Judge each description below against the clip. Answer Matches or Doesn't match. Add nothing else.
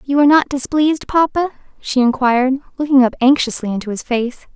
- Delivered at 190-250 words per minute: Doesn't match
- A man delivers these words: Doesn't match